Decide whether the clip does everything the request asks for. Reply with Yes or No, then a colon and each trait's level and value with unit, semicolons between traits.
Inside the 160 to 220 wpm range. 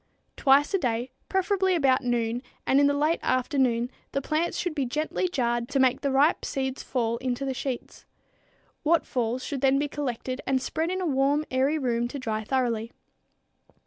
Yes: average, 180 wpm